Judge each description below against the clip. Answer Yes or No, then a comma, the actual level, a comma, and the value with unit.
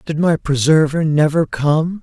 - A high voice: No, medium, 155 Hz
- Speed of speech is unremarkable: Yes, average, 150 wpm